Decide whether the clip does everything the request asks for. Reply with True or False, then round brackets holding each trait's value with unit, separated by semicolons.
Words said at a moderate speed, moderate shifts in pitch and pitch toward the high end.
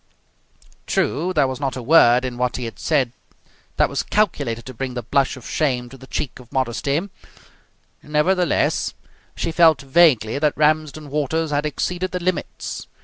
False (165 wpm; 3.7 semitones; 140 Hz)